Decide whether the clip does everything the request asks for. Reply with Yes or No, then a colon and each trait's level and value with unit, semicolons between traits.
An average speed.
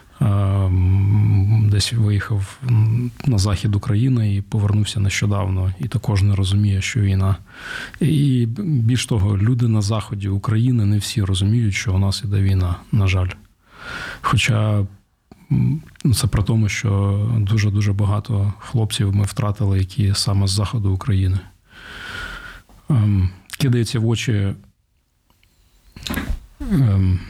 Yes: average, 115 wpm